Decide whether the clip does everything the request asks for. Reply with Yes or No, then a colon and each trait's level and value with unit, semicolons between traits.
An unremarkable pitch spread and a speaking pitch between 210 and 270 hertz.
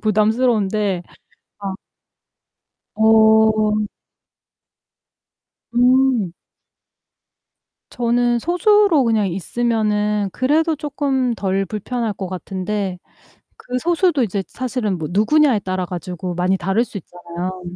Yes: average, 4.6 semitones; high, 215 Hz